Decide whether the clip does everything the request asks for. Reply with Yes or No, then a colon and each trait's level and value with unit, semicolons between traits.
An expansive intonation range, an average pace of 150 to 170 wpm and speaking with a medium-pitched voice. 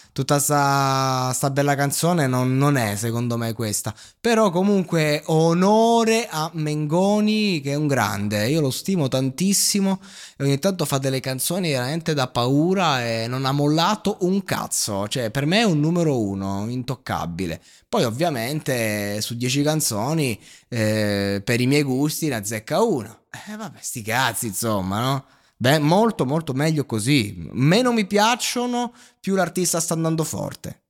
Yes: wide, 6.1 semitones; average, 155 wpm; medium, 145 Hz